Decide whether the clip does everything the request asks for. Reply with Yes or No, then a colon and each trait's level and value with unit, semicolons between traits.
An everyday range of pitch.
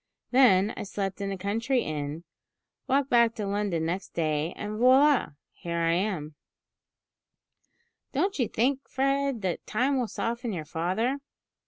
No: wide, 6.7 semitones